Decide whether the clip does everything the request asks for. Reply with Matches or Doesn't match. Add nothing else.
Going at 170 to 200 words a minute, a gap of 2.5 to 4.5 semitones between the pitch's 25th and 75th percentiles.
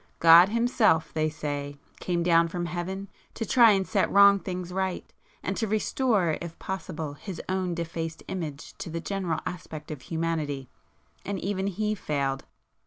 Doesn't match